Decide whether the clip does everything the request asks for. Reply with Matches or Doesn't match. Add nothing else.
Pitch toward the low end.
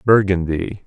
Matches